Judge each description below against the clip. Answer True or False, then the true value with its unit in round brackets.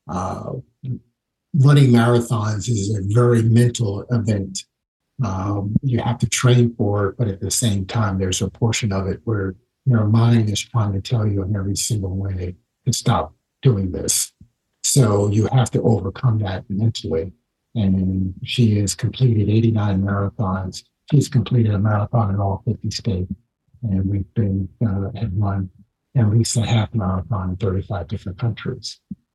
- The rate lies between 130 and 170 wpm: True (160 wpm)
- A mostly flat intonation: False (3.4 semitones)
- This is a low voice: True (105 Hz)